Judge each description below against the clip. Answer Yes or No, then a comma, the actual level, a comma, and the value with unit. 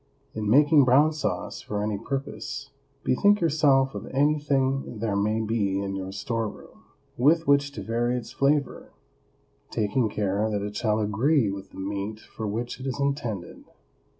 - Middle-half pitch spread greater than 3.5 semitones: Yes, average, 5.1 semitones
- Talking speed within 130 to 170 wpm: Yes, average, 160 wpm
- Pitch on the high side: No, low, 115 Hz